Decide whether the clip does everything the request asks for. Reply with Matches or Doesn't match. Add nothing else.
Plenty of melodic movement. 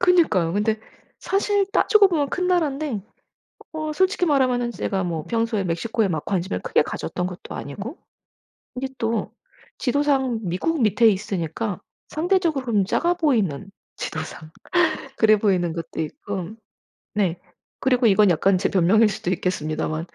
Matches